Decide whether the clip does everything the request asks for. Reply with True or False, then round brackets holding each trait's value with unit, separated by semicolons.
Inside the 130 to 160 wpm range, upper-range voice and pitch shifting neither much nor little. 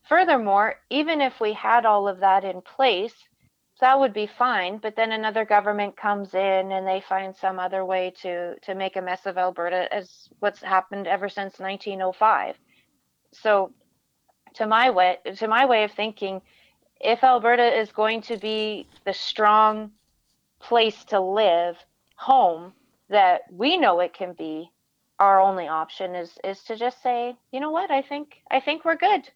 False (170 wpm; 210 Hz; 4.2 semitones)